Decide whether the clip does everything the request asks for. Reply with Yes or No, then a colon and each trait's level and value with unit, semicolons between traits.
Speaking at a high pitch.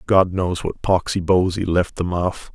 No: very low, 90 Hz